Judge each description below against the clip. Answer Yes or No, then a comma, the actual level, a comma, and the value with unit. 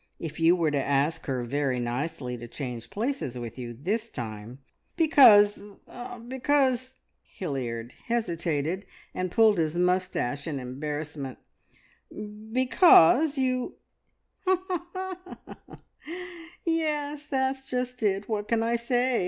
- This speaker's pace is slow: Yes, slow, 120 wpm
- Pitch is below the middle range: No, medium, 185 Hz